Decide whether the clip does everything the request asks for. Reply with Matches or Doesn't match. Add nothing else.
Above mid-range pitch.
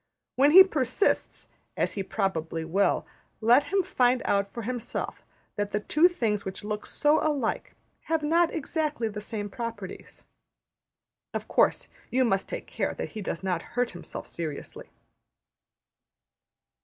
Matches